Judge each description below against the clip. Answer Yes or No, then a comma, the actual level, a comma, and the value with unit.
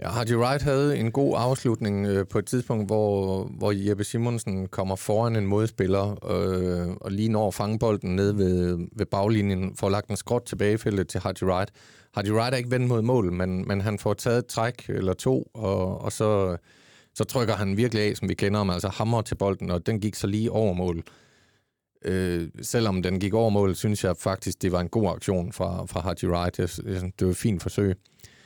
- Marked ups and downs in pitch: No, average, 3.2 semitones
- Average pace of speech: Yes, average, 210 wpm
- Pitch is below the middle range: Yes, low, 100 Hz